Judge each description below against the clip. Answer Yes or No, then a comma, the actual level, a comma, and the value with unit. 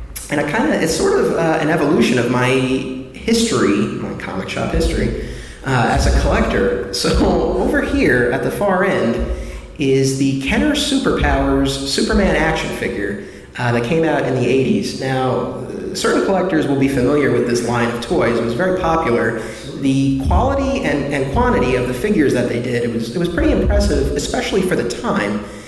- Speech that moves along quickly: No, average, 180 wpm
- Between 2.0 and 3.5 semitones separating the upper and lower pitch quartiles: Yes, average, 2.8 semitones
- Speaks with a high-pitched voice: No, low, 130 Hz